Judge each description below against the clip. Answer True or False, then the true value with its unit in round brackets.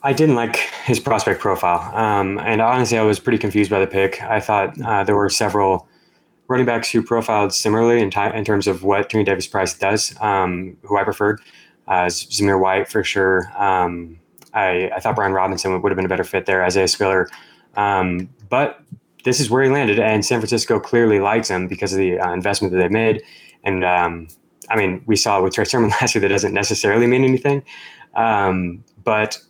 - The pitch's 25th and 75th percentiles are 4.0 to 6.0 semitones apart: False (2.9 semitones)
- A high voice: False (100 Hz)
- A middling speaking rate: False (210 wpm)